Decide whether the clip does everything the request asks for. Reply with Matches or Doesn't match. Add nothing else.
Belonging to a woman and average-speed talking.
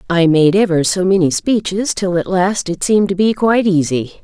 Doesn't match